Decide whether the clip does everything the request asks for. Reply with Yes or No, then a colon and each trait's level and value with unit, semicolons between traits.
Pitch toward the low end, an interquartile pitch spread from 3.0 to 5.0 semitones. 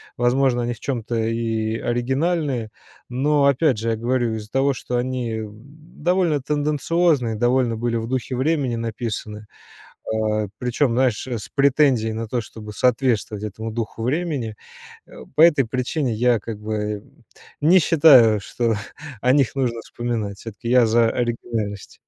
Yes: low, 120 Hz; average, 3.3 semitones